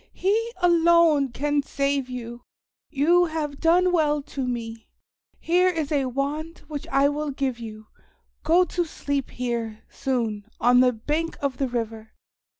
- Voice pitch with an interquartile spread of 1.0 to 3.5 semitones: No, average, 4.8 semitones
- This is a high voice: Yes, very high, 280 Hz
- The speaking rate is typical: Yes, average, 150 wpm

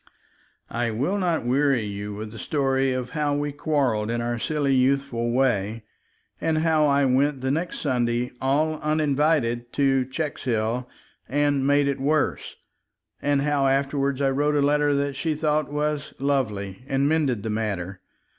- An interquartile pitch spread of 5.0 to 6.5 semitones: No, average, 3.4 semitones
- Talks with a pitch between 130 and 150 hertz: Yes, low, 135 Hz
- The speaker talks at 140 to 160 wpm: Yes, average, 155 wpm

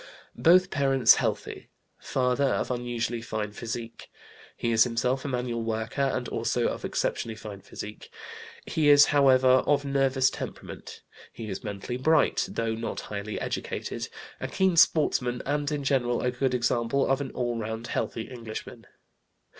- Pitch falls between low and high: No, low, 125 Hz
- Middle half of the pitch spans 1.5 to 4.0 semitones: Yes, average, 3.1 semitones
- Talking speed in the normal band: Yes, average, 150 wpm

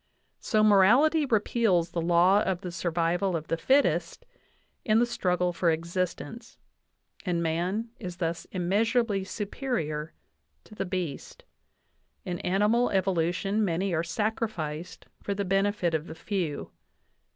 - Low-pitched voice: No, medium, 185 Hz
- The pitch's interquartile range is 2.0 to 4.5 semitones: Yes, average, 3.8 semitones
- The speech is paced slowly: Yes, slow, 130 wpm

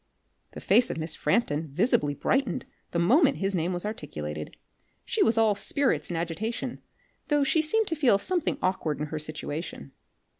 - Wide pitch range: Yes, wide, 8.7 semitones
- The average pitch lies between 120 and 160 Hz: No, high, 195 Hz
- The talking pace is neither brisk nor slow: Yes, average, 165 wpm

